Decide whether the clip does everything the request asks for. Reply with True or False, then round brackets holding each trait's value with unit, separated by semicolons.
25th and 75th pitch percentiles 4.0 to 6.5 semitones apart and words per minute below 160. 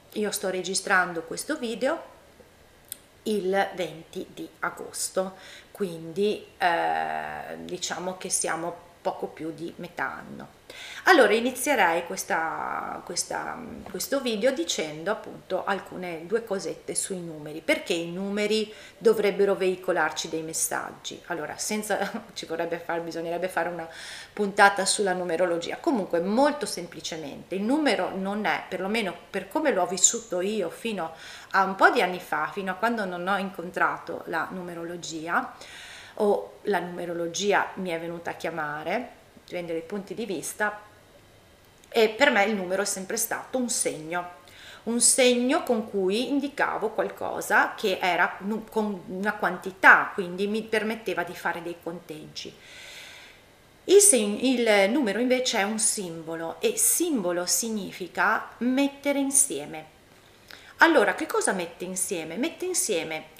True (5.0 semitones; 130 wpm)